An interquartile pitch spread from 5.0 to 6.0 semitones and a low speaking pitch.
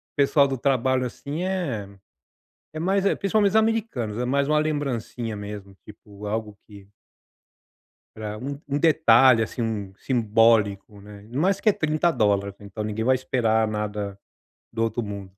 Yes: wide, 5.5 semitones; low, 115 Hz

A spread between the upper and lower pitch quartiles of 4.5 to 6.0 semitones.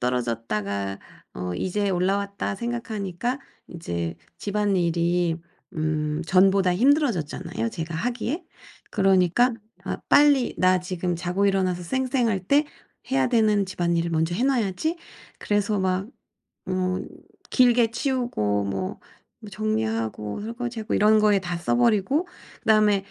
Yes: average, 5.3 semitones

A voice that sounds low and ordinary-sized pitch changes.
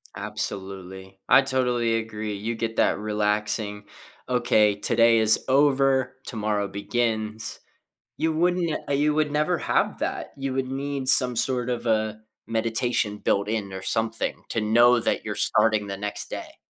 Yes: low, 115 Hz; average, 3.7 semitones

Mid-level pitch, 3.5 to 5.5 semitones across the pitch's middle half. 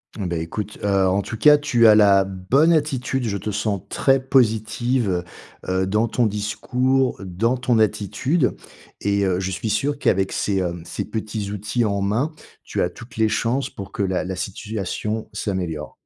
No: low, 105 Hz; average, 4.1 semitones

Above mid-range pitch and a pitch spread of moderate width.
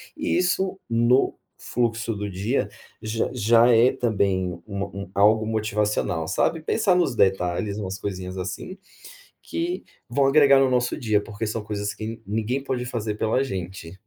No: low, 110 Hz; average, 3.7 semitones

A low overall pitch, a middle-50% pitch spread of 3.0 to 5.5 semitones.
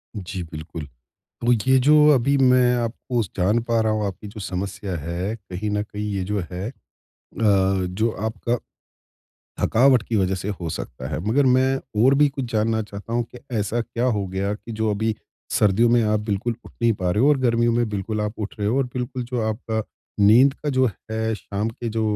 Yes: low, 110 Hz; average, 3.3 semitones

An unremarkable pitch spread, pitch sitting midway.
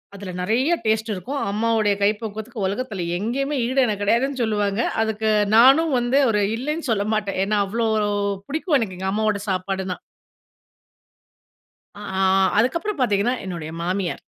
No: average, 4.1 semitones; high, 220 Hz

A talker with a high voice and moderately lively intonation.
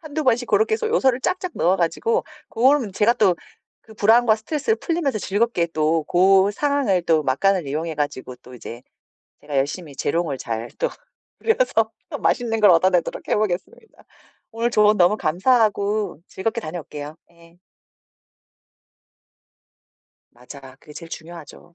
No: high, 195 Hz; wide, 6.7 semitones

